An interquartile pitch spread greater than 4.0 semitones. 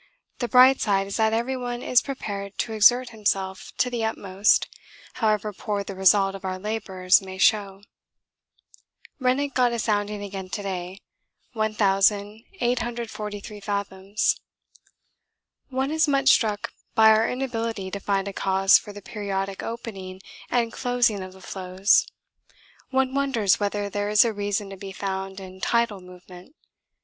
No: average, 3.2 semitones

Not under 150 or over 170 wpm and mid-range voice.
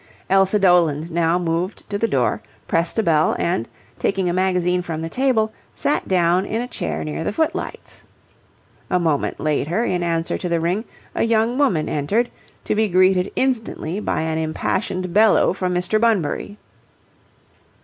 Yes: average, 160 wpm; medium, 180 Hz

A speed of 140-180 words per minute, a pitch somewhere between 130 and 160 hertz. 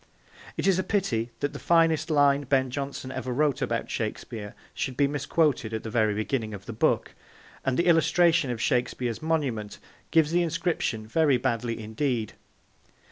Yes: average, 165 wpm; low, 135 Hz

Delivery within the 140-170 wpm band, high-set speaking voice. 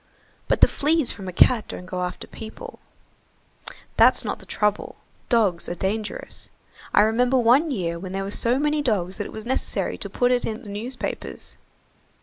No: average, 180 wpm; high, 220 Hz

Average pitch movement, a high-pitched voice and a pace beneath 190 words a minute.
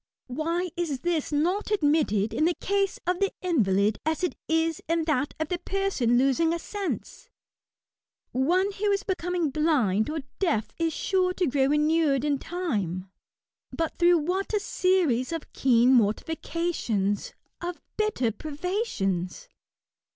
No: wide, 5.8 semitones; very high, 320 Hz; average, 140 wpm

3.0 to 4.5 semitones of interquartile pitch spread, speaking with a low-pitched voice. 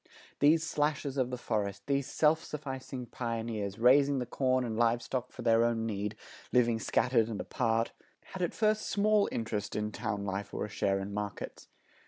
Yes: average, 4.2 semitones; low, 120 Hz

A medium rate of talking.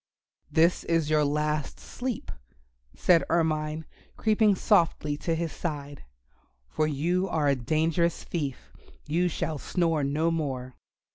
No: slow, 125 wpm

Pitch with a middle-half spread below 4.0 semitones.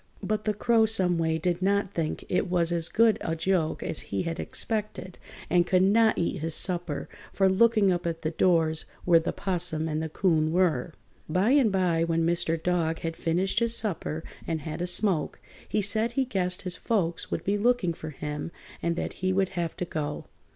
Yes: average, 3.3 semitones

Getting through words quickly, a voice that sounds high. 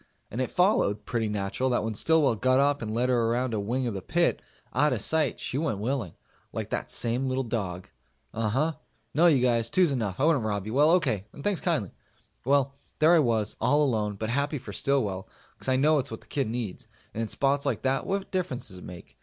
No: fast, 230 wpm; low, 125 Hz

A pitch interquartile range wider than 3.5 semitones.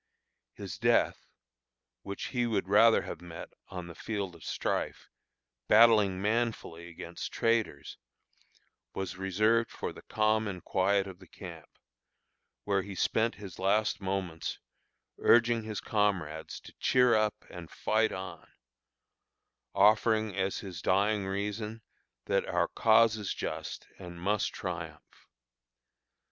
No: average, 3.1 semitones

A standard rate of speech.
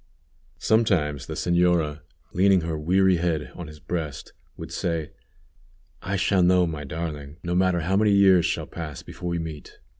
Yes: average, 160 wpm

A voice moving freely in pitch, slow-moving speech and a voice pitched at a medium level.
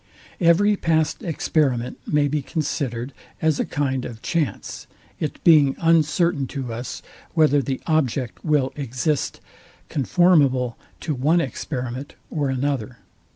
No: average, 3.5 semitones; slow, 125 wpm; medium, 145 Hz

